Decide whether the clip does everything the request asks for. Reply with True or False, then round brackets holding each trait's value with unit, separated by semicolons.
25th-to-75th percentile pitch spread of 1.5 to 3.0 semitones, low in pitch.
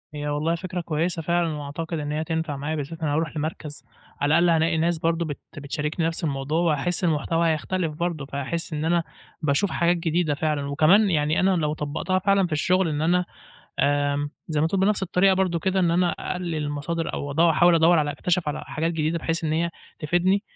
False (2.6 semitones; 165 Hz)